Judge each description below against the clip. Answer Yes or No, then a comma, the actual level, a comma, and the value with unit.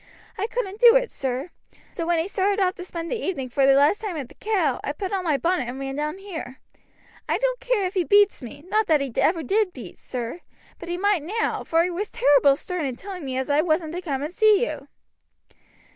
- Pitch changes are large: Yes, wide, 6.1 semitones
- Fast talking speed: Yes, fast, 240 wpm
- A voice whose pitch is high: Yes, very high, 345 Hz